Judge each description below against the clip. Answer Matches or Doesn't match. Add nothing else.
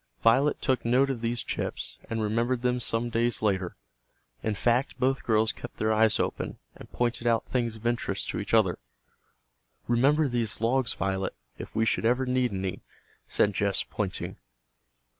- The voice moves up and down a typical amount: Doesn't match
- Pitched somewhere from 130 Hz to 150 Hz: Doesn't match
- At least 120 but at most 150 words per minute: Doesn't match